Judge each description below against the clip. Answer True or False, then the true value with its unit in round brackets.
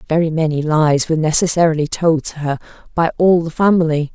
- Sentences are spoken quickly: False (160 wpm)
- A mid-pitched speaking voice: True (160 Hz)